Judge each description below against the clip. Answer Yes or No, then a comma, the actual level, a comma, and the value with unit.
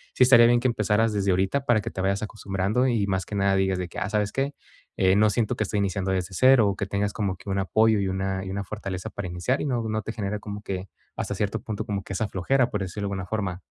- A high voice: No, low, 100 Hz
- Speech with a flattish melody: Yes, narrow, 2.3 semitones